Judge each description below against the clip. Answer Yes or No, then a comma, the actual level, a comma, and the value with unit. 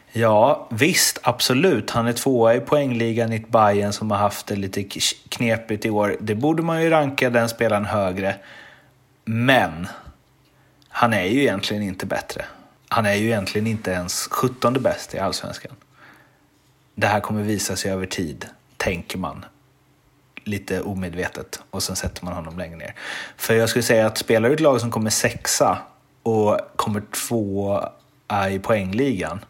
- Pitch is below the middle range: Yes, low, 105 Hz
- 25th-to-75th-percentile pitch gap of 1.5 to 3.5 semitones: Yes, average, 3.0 semitones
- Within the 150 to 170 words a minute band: Yes, average, 160 wpm